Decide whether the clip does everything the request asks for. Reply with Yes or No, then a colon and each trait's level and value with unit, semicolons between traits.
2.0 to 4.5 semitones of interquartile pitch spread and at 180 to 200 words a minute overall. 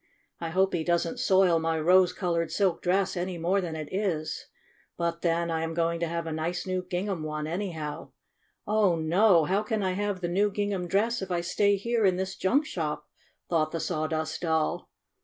Yes: average, 2.8 semitones; average, 195 wpm